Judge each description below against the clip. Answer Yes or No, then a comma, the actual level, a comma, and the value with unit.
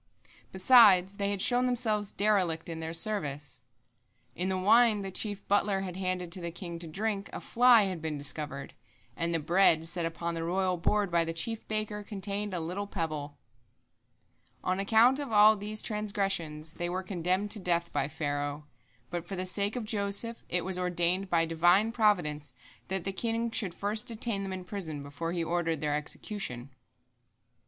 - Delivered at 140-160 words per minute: No, average, 180 wpm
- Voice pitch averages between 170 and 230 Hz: Yes, medium, 185 Hz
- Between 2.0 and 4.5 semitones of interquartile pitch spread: Yes, average, 4.0 semitones